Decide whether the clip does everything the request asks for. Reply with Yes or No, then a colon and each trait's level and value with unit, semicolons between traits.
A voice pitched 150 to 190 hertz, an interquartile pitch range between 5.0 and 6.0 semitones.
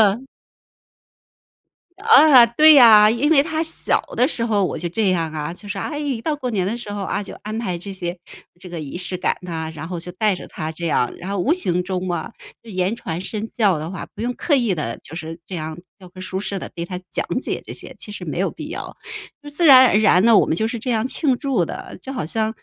No: high, 200 Hz; wide, 5.4 semitones